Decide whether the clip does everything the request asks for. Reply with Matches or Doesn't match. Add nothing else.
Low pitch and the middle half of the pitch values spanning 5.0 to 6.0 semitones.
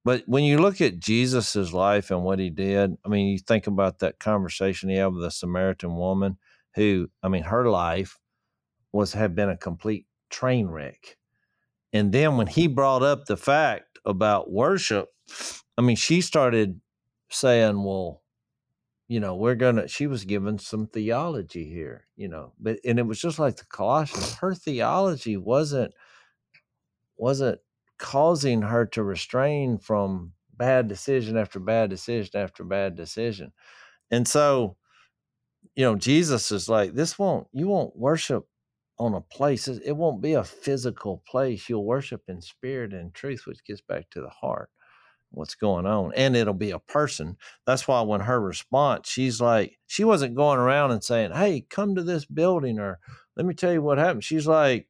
Matches